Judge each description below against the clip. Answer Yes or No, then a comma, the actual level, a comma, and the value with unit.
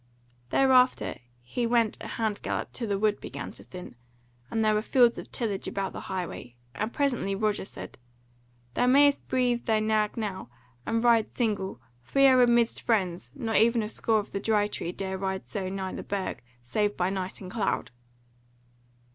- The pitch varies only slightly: No, average, 3.4 semitones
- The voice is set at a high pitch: Yes, high, 215 Hz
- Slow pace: No, average, 180 wpm